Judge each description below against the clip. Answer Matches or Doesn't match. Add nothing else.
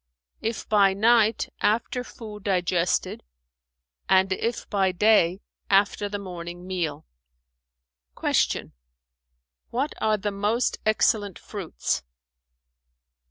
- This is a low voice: Doesn't match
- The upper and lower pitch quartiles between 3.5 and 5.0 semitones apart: Doesn't match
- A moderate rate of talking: Doesn't match